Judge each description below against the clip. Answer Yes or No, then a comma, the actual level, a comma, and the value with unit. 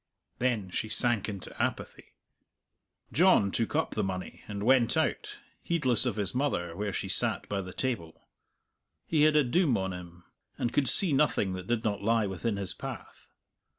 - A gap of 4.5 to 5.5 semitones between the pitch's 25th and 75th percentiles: Yes, average, 5.2 semitones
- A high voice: No, low, 110 Hz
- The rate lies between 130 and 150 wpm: No, average, 175 wpm